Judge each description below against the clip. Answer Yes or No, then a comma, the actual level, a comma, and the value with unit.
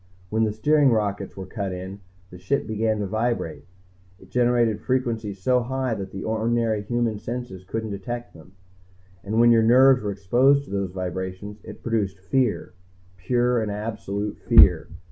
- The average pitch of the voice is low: Yes, low, 110 Hz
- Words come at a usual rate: Yes, average, 160 wpm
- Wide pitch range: No, average, 3.4 semitones